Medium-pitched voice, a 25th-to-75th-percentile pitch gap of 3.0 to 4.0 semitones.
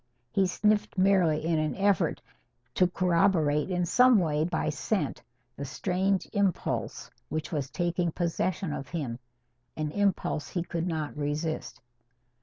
Yes: medium, 170 Hz; average, 3.7 semitones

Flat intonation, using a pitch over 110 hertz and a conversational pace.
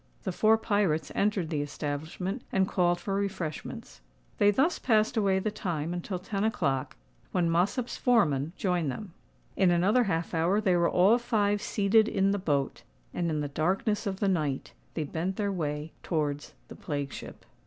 No: average, 4.5 semitones; medium, 185 Hz; average, 175 wpm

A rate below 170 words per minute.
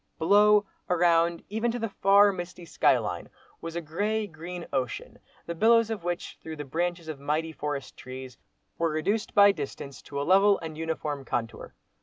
No: average, 175 wpm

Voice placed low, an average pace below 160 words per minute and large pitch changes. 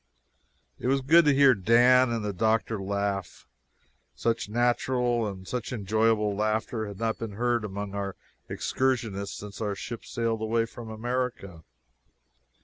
No: low, 110 Hz; average, 140 wpm; average, 3.0 semitones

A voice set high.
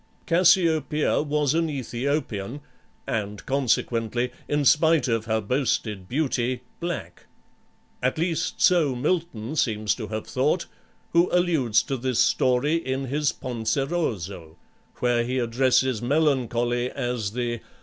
No: low, 130 Hz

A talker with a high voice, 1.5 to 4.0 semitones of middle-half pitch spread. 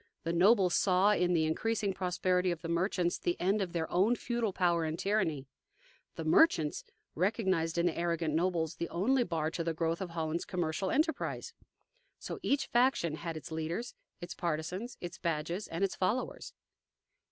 No: medium, 175 Hz; average, 3.0 semitones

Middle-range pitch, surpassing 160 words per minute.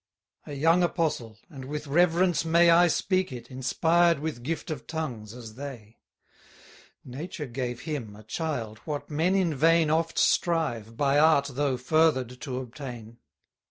No: medium, 145 Hz; average, 150 wpm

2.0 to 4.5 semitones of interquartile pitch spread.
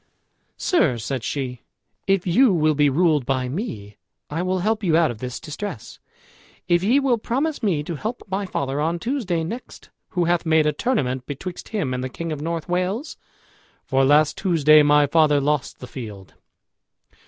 No: wide, 5.4 semitones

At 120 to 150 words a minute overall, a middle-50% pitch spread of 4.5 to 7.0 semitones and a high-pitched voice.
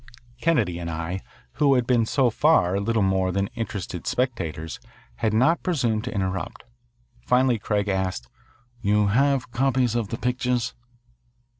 No: average, 140 wpm; average, 4.8 semitones; low, 115 Hz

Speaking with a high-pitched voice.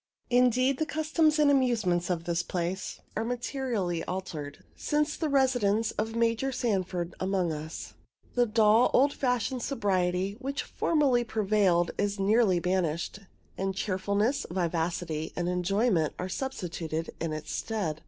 Yes: high, 200 Hz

